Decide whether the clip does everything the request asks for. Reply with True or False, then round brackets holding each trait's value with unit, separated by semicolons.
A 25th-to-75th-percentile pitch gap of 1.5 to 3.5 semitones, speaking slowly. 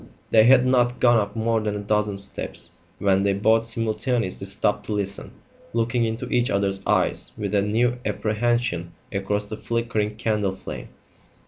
False (2.5 semitones; 160 wpm)